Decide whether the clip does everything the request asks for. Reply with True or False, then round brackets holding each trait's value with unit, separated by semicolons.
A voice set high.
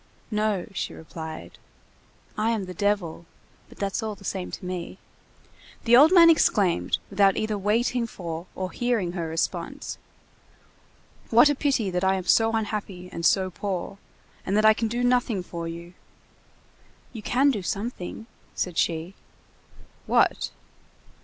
True (200 Hz)